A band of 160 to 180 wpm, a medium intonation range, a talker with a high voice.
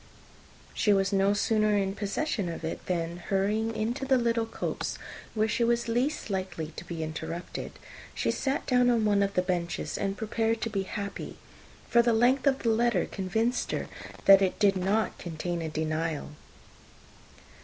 Yes: average, 170 wpm; average, 4.0 semitones; high, 205 Hz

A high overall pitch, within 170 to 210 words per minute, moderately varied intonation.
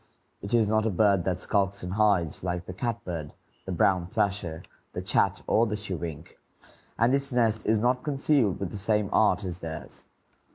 No: low, 100 Hz; average, 180 wpm; average, 3.6 semitones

